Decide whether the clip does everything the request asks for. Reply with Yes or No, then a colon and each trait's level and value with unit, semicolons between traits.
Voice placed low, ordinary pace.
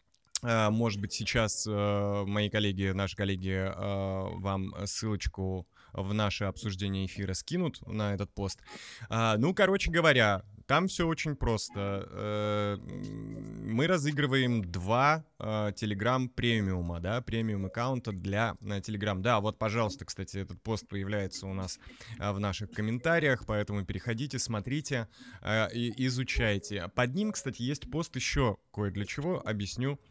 Yes: low, 105 Hz; average, 135 wpm